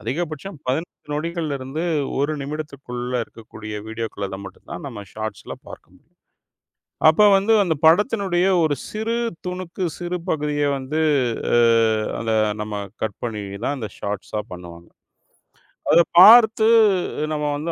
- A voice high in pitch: No, medium, 145 Hz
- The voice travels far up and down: Yes, wide, 7.8 semitones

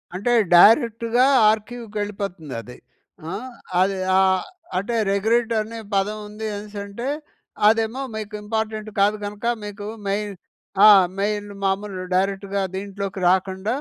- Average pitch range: No, narrow, 2.0 semitones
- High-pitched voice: Yes, high, 205 Hz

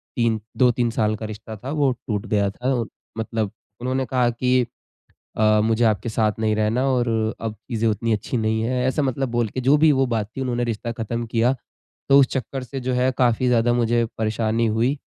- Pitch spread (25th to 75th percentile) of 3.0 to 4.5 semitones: No, narrow, 2.4 semitones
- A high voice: No, low, 120 Hz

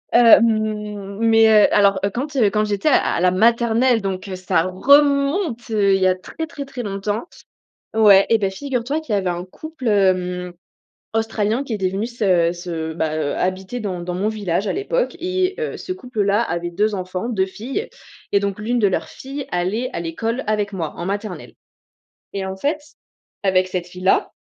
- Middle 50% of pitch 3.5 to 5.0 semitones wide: Yes, average, 4.3 semitones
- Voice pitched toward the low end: No, high, 205 Hz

